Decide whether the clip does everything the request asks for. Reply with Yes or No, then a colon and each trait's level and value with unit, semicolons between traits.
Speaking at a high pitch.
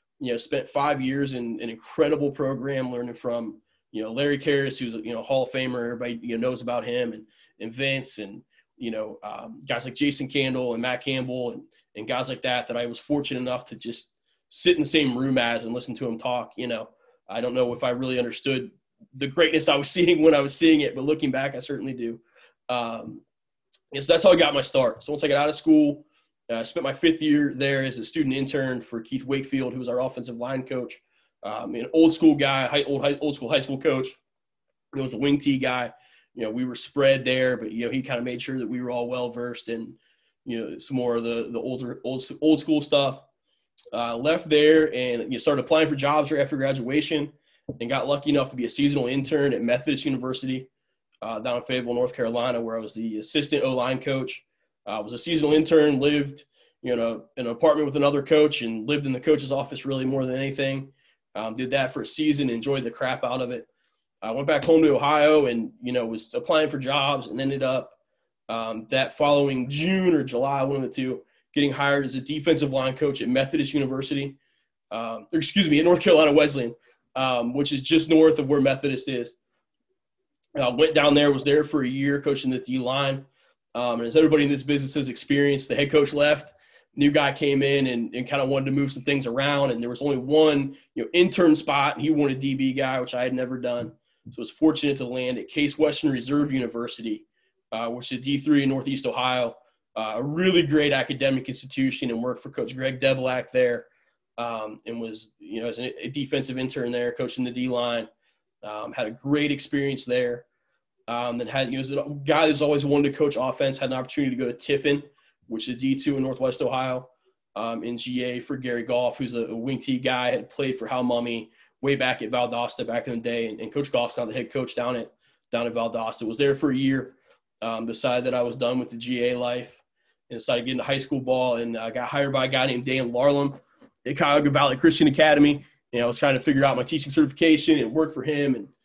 No: low, 135 Hz